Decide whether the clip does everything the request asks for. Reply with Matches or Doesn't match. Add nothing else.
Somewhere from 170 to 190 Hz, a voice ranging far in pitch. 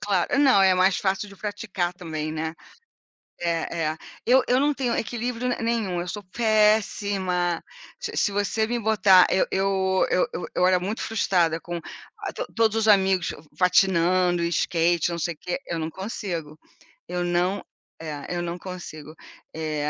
Doesn't match